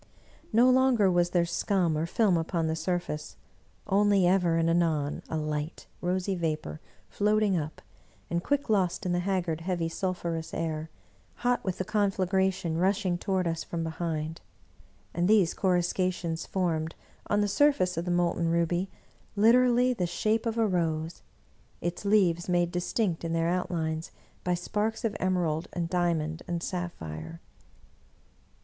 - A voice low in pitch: No, medium, 175 Hz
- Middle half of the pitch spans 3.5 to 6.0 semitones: No, average, 2.8 semitones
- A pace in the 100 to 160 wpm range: Yes, average, 145 wpm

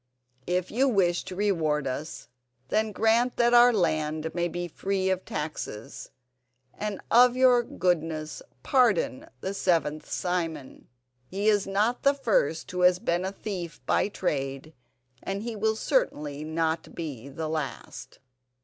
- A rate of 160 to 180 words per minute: No, average, 140 wpm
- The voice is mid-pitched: Yes, medium, 180 Hz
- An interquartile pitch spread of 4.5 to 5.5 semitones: Yes, average, 5.2 semitones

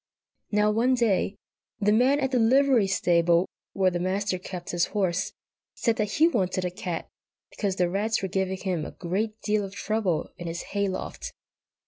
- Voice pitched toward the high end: Yes, high, 195 Hz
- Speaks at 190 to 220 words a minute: No, average, 180 wpm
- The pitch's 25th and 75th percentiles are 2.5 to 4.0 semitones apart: Yes, average, 3.3 semitones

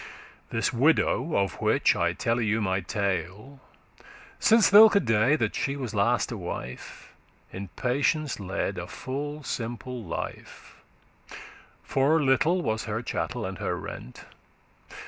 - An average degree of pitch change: No, wide, 5.9 semitones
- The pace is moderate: No, slow, 130 wpm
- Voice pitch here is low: Yes, low, 120 Hz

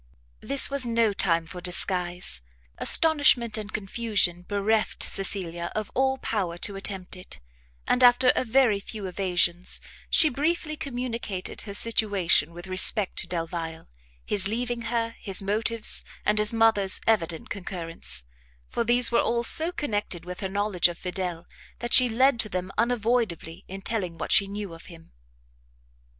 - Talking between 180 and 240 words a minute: No, average, 150 wpm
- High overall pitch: Yes, high, 205 Hz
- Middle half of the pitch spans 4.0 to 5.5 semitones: Yes, average, 4.5 semitones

